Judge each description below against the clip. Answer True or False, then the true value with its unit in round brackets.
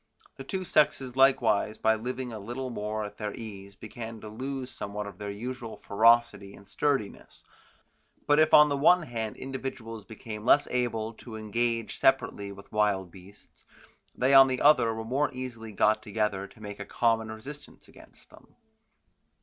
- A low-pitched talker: True (115 Hz)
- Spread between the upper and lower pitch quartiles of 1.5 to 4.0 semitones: True (3.7 semitones)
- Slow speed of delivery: False (165 wpm)